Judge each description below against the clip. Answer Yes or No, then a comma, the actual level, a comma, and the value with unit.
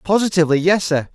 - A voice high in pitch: No, medium, 175 Hz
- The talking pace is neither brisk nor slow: Yes, average, 155 wpm